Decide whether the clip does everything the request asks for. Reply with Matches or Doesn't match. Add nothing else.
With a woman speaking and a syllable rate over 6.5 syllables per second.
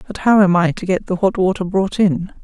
Doesn't match